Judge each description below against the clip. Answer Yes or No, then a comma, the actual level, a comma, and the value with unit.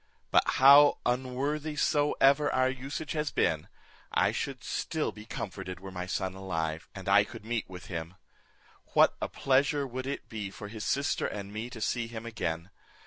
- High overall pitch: No, low, 115 Hz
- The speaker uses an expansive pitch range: Yes, wide, 6.2 semitones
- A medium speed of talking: Yes, average, 175 wpm